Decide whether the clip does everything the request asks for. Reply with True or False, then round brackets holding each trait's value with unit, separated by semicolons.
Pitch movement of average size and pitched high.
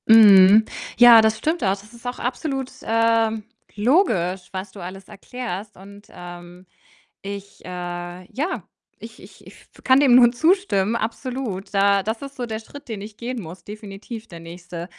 True (4.2 semitones; 215 Hz)